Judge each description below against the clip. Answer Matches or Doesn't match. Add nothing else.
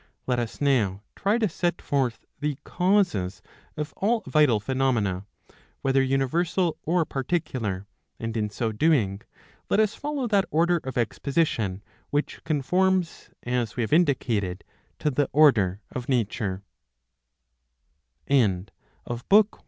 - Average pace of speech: Doesn't match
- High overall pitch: Doesn't match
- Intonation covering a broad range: Matches